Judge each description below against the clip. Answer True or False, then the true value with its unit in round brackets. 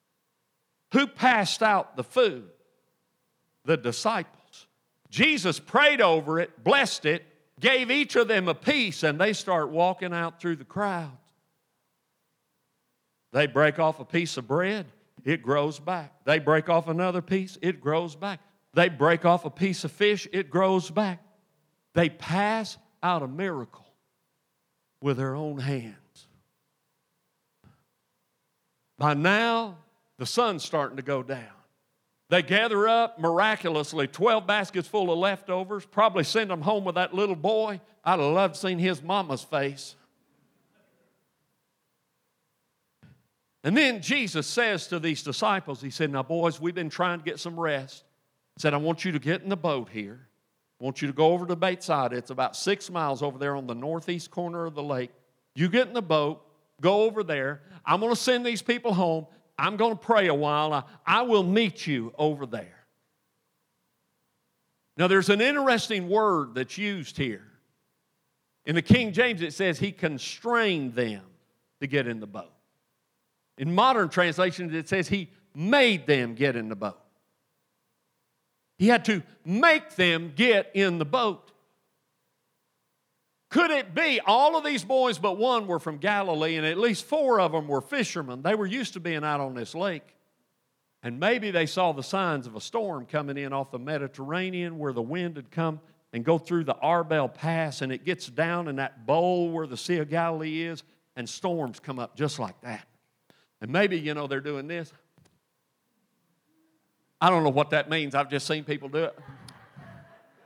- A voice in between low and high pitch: True (170 Hz)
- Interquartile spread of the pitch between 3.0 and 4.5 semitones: False (5.1 semitones)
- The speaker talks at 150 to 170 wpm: True (165 wpm)